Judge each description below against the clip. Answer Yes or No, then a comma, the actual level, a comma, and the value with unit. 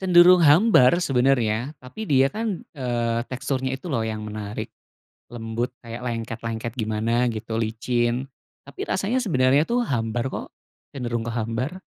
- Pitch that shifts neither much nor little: Yes, average, 3.5 semitones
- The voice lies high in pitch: No, low, 125 Hz